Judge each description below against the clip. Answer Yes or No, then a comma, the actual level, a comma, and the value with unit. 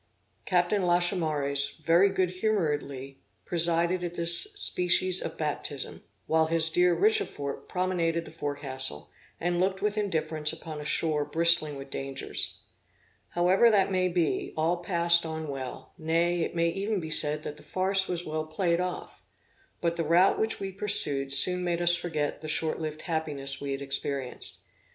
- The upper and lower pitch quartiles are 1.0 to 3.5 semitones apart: Yes, average, 3.1 semitones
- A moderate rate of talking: Yes, average, 160 wpm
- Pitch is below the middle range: No, medium, 165 Hz